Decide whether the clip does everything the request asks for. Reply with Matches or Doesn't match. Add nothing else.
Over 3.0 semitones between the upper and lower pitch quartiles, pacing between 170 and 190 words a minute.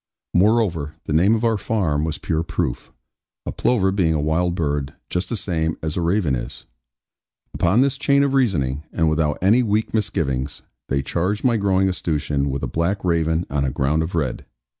Matches